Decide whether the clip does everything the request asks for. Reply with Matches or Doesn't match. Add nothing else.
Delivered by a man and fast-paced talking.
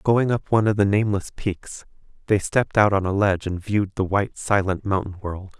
Matches